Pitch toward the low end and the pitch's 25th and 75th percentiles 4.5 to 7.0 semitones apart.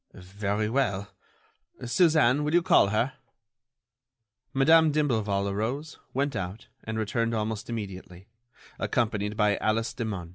Yes: low, 110 Hz; average, 5.0 semitones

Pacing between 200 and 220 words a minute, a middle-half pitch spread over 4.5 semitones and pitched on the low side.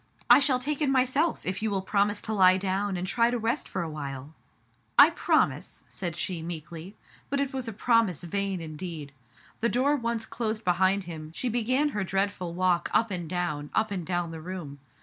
No: fast, 205 wpm; average, 5.1 semitones; high, 195 Hz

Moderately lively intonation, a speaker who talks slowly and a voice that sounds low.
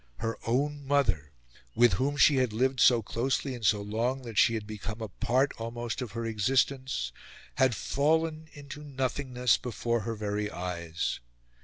No: average, 3.8 semitones; average, 160 wpm; low, 120 Hz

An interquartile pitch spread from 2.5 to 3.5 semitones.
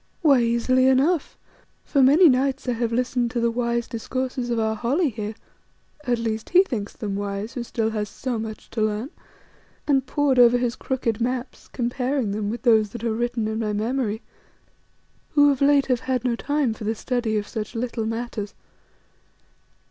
Yes: average, 2.8 semitones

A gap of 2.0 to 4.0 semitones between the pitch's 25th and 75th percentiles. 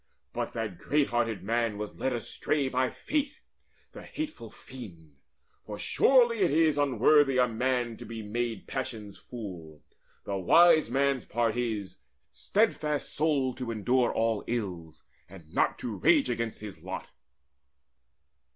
No: average, 4.7 semitones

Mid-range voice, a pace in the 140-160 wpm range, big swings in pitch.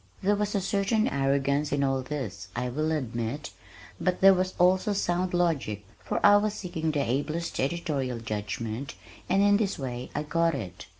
No: medium, 150 Hz; average, 175 wpm; wide, 6.3 semitones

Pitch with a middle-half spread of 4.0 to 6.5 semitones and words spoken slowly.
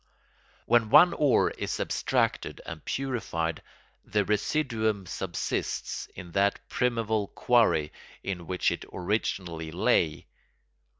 Yes: average, 5.1 semitones; slow, 105 wpm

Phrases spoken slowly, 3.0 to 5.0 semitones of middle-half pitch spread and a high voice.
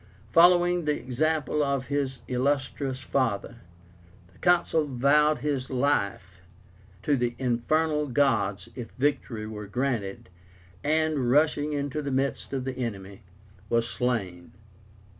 No: slow, 120 wpm; average, 3.9 semitones; low, 135 Hz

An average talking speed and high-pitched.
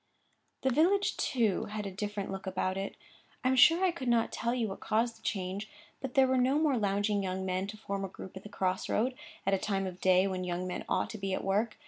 No: fast, 255 wpm; high, 205 Hz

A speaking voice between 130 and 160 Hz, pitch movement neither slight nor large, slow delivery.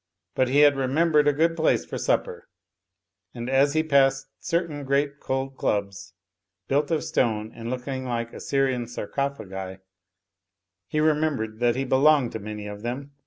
No: low, 135 Hz; average, 3.8 semitones; average, 155 wpm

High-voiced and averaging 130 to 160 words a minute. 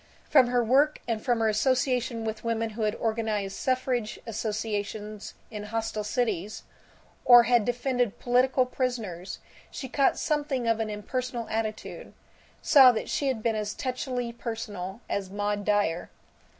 Yes: high, 225 Hz; average, 145 wpm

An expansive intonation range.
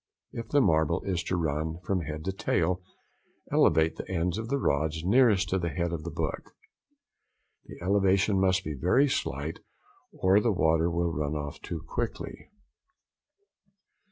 No: average, 3.4 semitones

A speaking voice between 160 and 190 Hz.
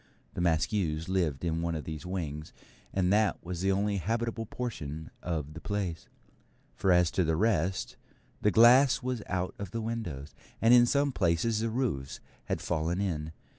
No: very low, 90 Hz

